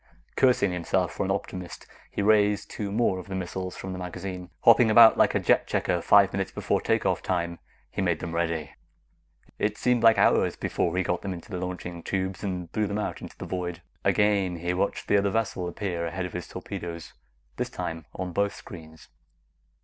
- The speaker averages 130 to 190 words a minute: No, average, 200 wpm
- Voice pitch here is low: Yes, very low, 95 Hz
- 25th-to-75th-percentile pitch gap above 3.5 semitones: No, narrow, 2.6 semitones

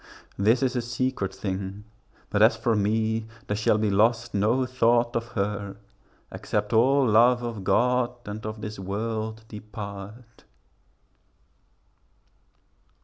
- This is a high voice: No, low, 110 Hz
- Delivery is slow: Yes, slow, 125 wpm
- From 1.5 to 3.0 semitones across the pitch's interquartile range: Yes, narrow, 2.4 semitones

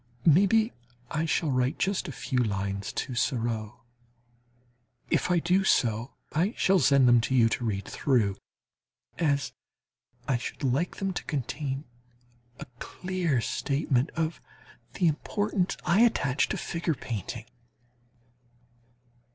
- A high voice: No, medium, 140 Hz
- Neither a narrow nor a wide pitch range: No, wide, 6.3 semitones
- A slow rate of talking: Yes, slow, 125 wpm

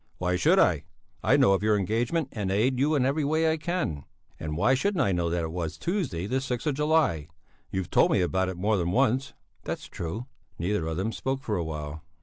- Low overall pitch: Yes, low, 105 Hz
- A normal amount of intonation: No, wide, 7.8 semitones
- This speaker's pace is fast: Yes, fast, 225 wpm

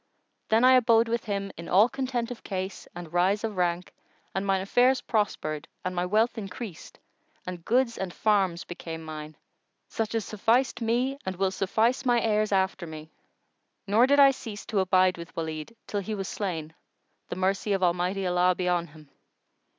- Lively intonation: No, average, 4.1 semitones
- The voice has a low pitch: No, high, 195 Hz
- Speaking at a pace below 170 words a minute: No, average, 180 wpm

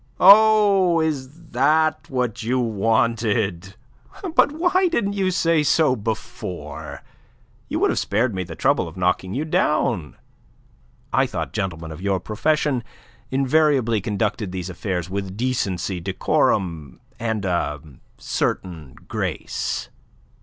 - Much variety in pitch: Yes, wide, 8.5 semitones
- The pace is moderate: No, slow, 120 wpm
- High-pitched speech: No, low, 115 Hz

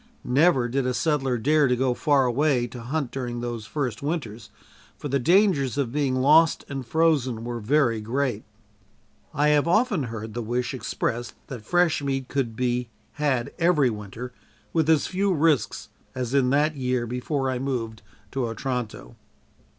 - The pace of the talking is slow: No, average, 165 wpm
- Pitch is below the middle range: Yes, low, 130 Hz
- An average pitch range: Yes, average, 3.7 semitones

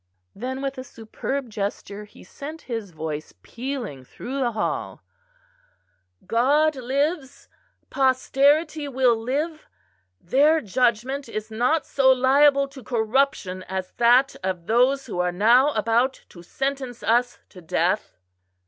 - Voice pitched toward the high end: Yes, very high, 250 Hz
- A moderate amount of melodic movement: Yes, average, 4.3 semitones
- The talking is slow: Yes, slow, 125 wpm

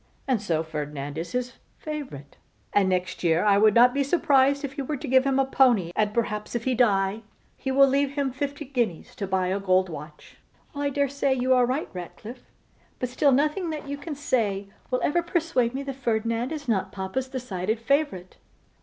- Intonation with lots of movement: Yes, wide, 6.1 semitones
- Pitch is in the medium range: No, very high, 250 Hz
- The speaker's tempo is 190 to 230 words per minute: Yes, average, 200 wpm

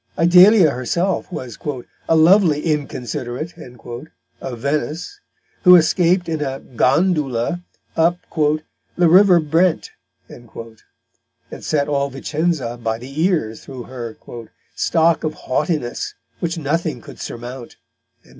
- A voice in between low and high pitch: Yes, medium, 150 Hz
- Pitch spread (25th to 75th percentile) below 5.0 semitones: No, average, 5.3 semitones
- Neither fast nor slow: No, slow, 110 wpm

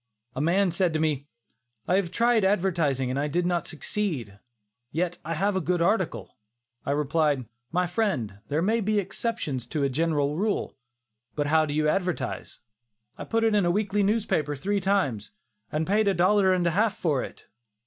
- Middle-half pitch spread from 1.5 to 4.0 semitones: No, average, 5.2 semitones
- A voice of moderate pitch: Yes, medium, 175 Hz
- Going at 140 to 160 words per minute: No, average, 180 wpm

